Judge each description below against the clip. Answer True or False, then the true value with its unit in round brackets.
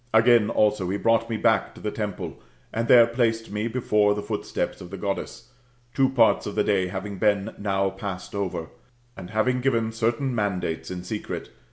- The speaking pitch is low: True (105 Hz)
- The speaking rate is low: False (185 wpm)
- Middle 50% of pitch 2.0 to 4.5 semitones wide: True (2.8 semitones)